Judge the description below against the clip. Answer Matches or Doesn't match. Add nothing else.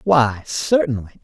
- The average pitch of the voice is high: Doesn't match